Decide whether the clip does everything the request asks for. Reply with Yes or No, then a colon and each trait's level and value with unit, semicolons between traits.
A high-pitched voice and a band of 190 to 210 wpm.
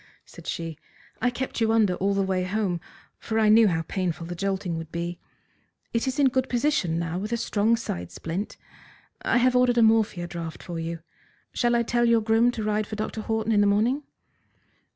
Yes: high, 210 Hz; fast, 205 wpm